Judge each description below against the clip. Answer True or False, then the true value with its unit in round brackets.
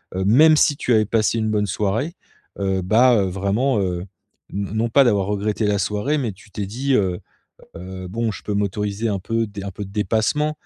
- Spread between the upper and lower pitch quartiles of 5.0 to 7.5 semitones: False (2.9 semitones)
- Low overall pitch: True (105 Hz)